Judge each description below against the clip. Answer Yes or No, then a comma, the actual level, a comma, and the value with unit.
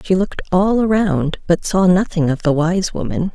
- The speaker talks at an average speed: Yes, average, 195 wpm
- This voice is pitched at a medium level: Yes, medium, 180 Hz